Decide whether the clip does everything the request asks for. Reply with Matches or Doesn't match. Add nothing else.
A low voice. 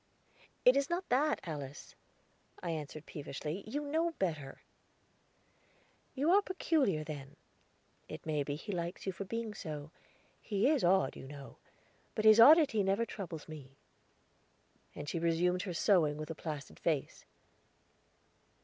Doesn't match